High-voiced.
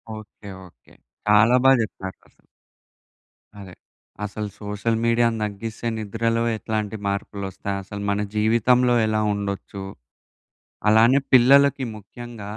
No: low, 110 Hz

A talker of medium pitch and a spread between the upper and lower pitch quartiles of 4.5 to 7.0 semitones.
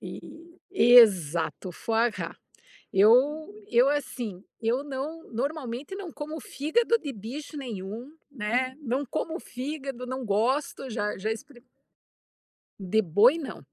No: very high, 250 Hz; average, 4.8 semitones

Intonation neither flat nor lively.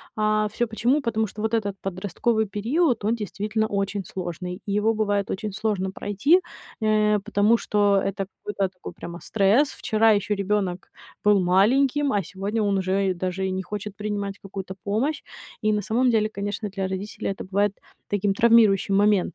No: narrow, 1.9 semitones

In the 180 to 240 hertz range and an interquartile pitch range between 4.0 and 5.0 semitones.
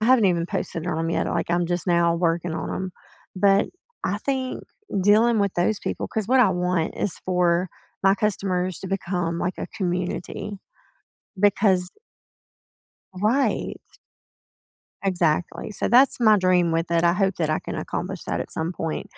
No: medium, 185 Hz; average, 3.0 semitones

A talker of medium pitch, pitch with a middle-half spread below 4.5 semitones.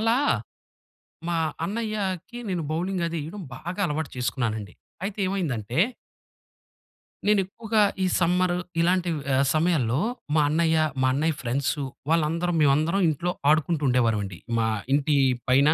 No: medium, 165 Hz; average, 5.0 semitones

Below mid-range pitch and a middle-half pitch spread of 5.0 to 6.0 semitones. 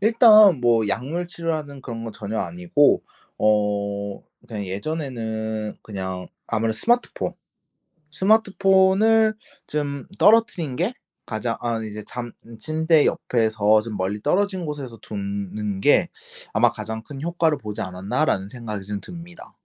No: low, 120 Hz; wide, 8.1 semitones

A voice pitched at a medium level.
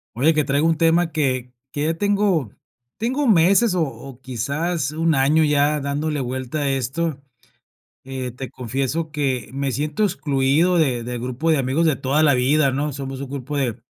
Yes: medium, 145 Hz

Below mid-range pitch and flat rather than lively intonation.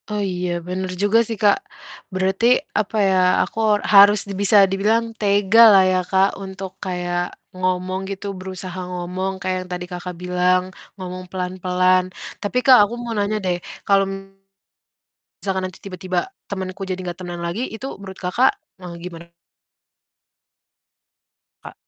No: high, 190 Hz; narrow, 1.7 semitones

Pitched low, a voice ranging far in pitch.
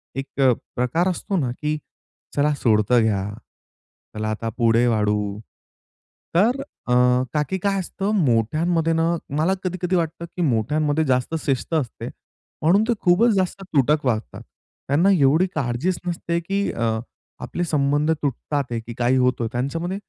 No: medium, 150 Hz; wide, 6.1 semitones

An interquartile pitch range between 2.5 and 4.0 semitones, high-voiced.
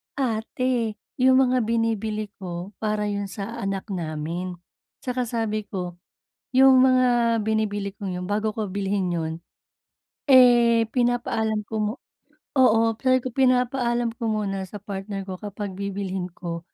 Yes: average, 3.4 semitones; high, 215 Hz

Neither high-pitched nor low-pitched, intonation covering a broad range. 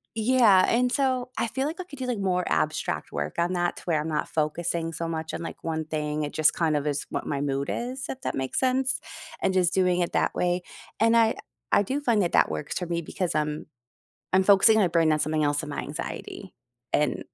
Yes: medium, 175 Hz; wide, 6.6 semitones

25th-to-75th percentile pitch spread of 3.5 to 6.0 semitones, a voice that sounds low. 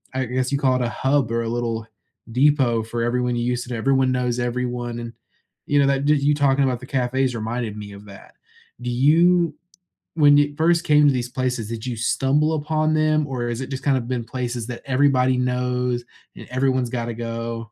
No: average, 2.8 semitones; low, 125 Hz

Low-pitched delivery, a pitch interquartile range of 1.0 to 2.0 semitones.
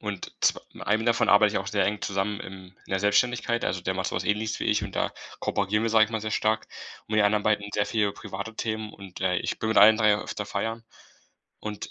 Yes: low, 105 Hz; narrow, 1.7 semitones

